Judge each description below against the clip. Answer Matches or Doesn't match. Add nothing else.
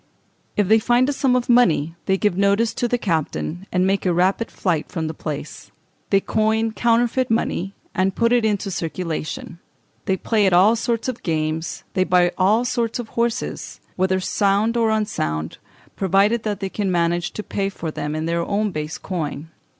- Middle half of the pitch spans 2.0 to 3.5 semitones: Doesn't match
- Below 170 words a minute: Doesn't match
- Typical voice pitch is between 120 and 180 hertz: Doesn't match